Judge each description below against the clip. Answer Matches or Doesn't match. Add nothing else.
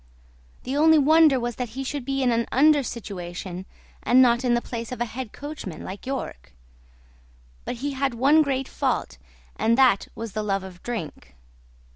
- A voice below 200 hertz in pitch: Doesn't match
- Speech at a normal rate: Matches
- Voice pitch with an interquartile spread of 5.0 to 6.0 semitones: Doesn't match